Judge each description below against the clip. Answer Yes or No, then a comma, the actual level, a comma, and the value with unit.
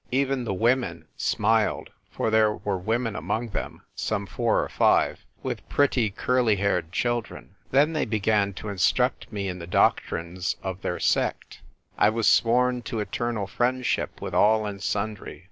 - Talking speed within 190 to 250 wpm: No, average, 165 wpm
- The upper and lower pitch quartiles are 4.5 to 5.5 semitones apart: No, average, 3.3 semitones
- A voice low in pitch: Yes, low, 110 Hz